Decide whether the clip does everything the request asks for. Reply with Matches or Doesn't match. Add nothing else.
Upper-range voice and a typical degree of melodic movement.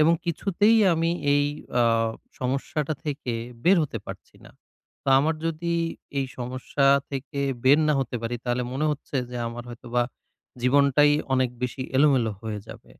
Doesn't match